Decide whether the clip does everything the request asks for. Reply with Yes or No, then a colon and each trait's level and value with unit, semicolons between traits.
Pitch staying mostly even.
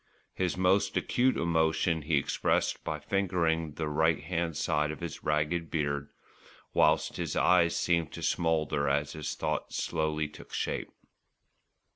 Yes: narrow, 2.1 semitones